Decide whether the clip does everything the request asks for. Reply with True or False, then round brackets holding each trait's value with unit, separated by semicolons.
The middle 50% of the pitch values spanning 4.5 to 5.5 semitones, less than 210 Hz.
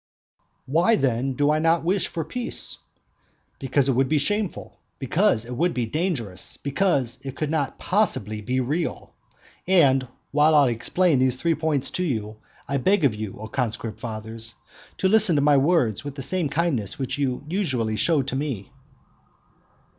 True (5.2 semitones; 140 Hz)